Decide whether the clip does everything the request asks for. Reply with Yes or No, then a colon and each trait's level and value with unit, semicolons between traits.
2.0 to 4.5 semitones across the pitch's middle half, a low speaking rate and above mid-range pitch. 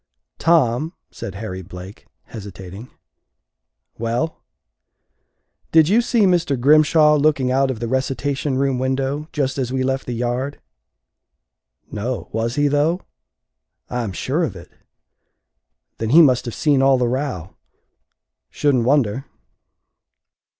No: average, 3.9 semitones; slow, 125 wpm; low, 130 Hz